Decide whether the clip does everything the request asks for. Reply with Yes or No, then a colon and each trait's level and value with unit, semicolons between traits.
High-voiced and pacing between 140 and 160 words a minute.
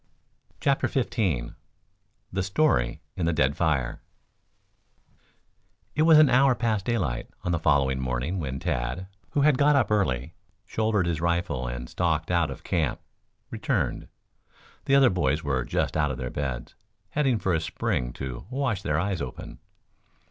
No: very low, 85 Hz; average, 155 wpm